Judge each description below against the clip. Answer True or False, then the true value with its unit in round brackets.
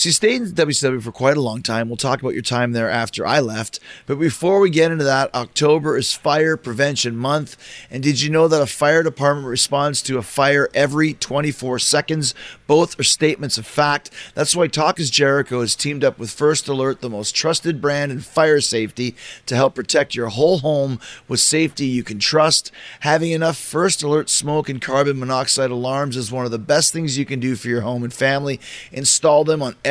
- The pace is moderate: False (215 wpm)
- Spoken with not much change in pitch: False (3.3 semitones)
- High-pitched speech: False (140 Hz)